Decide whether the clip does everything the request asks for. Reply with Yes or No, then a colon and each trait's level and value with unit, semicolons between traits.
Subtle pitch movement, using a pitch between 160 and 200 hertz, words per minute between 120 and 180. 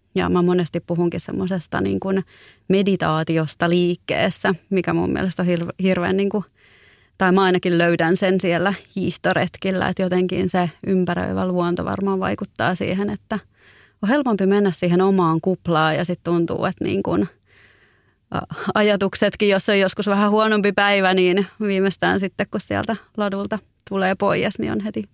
Yes: narrow, 2.3 semitones; medium, 185 Hz; average, 145 wpm